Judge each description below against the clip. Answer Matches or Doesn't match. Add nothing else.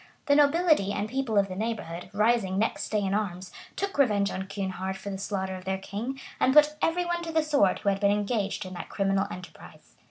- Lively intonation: Matches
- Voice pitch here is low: Doesn't match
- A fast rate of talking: Matches